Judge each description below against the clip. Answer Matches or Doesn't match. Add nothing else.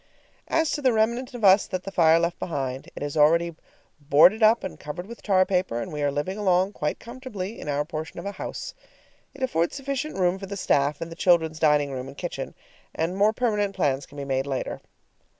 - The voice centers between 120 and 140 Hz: Doesn't match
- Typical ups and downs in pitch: Doesn't match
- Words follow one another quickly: Matches